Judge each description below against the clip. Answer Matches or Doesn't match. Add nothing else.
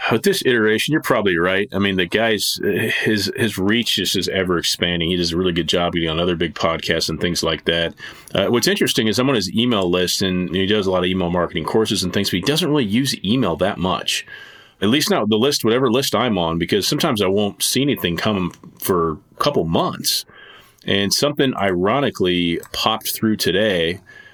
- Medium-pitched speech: Doesn't match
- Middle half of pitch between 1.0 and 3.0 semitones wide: Doesn't match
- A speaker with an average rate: Doesn't match